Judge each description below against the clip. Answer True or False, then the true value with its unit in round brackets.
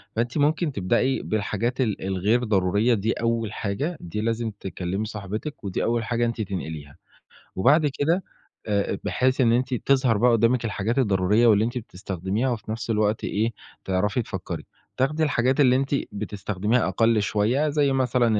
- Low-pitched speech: True (115 Hz)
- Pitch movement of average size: True (3.7 semitones)